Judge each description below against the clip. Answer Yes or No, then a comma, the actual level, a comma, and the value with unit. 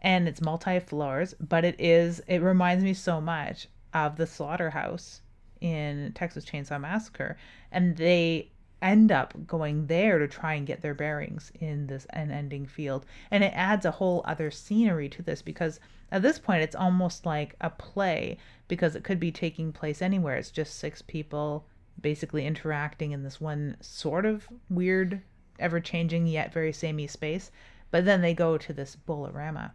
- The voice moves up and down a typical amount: Yes, average, 3.1 semitones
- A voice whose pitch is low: No, medium, 165 Hz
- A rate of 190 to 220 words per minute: No, average, 170 wpm